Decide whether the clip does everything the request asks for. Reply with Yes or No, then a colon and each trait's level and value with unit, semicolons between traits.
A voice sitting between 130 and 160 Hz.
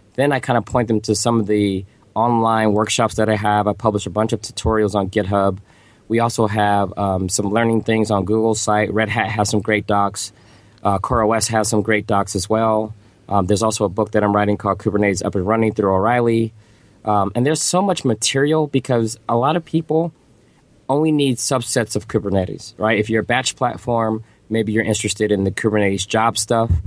No: low, 110 Hz